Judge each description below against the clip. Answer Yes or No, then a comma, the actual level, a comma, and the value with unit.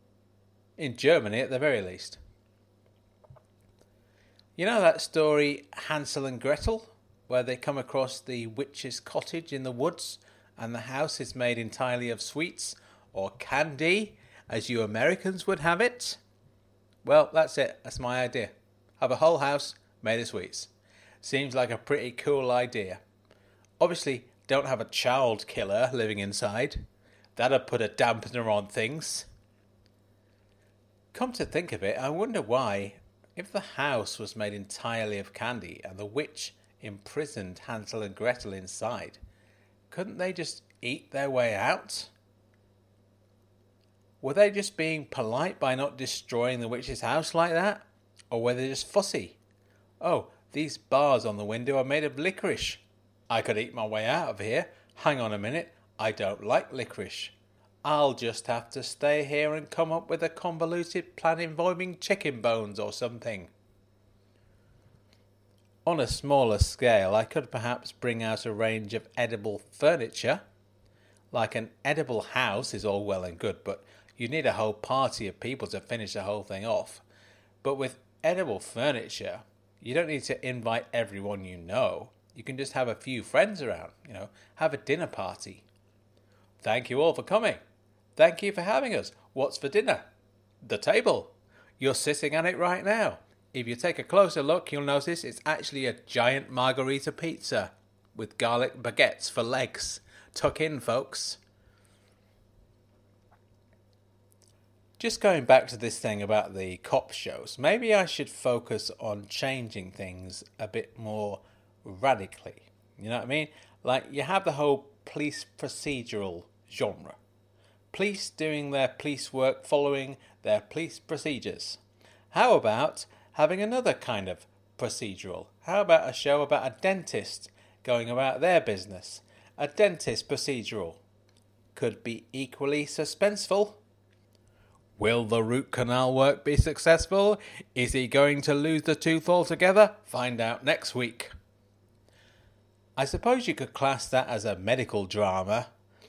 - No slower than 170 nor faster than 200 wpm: No, average, 150 wpm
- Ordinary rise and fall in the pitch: No, wide, 6.0 semitones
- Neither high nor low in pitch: No, low, 115 Hz